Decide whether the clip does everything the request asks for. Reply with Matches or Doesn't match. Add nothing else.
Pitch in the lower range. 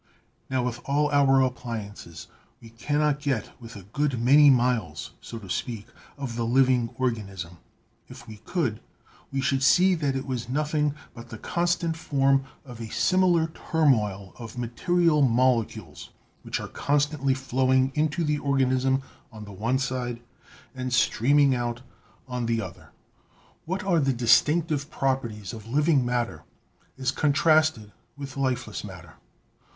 Matches